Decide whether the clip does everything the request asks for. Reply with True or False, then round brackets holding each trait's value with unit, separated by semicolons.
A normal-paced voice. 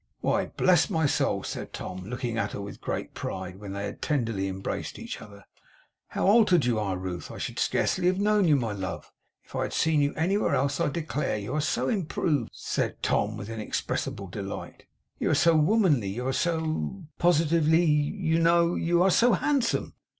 True (190 wpm)